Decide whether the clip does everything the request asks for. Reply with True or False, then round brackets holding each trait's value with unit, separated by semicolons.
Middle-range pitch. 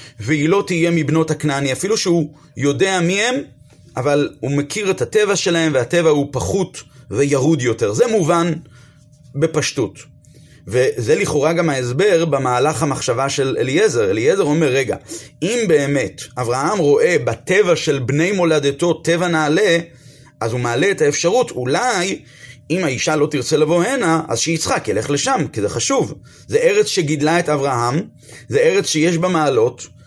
True (155 Hz)